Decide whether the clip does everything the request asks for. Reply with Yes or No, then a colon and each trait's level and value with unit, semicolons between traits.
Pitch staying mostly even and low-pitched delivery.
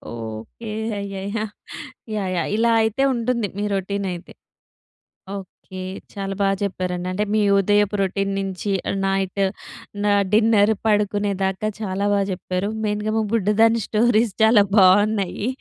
No: narrow, 1.9 semitones; high, 200 Hz